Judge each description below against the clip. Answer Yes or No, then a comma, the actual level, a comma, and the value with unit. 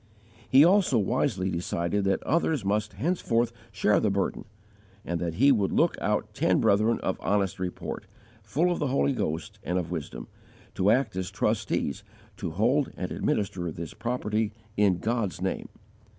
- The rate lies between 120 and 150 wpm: No, average, 160 wpm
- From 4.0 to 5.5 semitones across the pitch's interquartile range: Yes, average, 4.7 semitones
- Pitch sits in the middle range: No, low, 105 Hz